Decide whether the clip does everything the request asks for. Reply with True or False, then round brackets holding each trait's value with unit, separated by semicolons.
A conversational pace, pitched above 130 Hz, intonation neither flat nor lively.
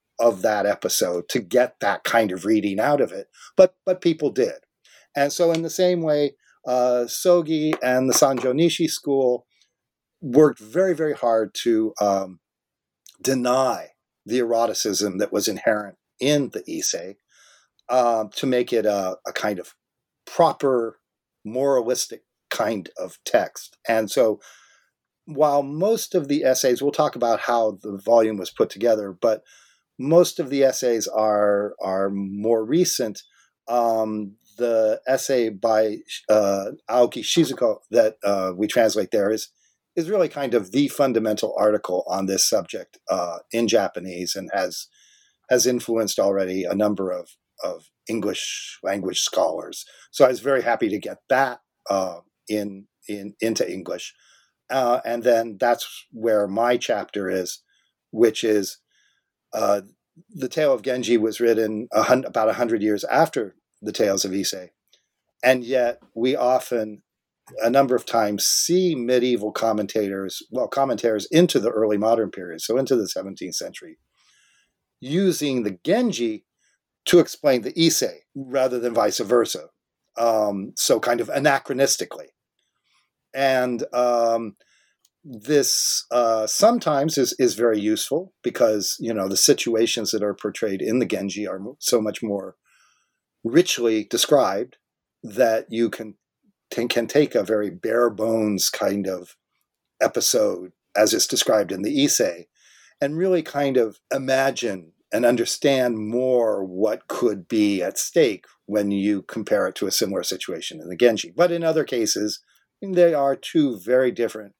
False (145 wpm; 120 Hz; 4.9 semitones)